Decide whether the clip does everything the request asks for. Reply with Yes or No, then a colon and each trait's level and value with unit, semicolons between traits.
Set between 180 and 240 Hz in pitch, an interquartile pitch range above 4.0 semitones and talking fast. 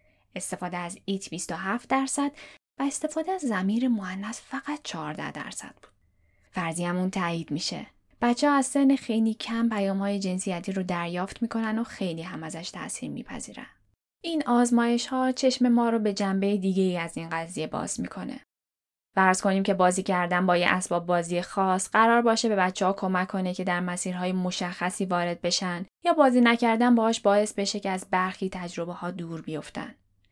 Yes: high, 190 Hz; average, 4.6 semitones; fast, 170 wpm